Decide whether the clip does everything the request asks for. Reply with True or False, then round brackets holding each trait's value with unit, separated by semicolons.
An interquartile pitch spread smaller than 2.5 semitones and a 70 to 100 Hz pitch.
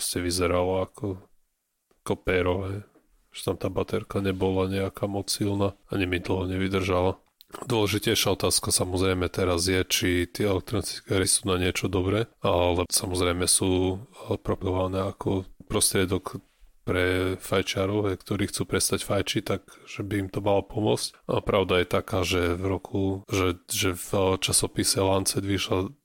True (1.6 semitones; 95 Hz)